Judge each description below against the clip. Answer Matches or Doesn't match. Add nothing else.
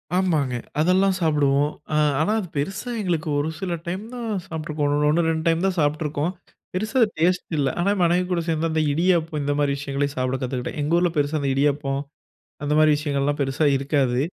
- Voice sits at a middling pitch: Matches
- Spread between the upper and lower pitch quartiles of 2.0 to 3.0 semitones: Doesn't match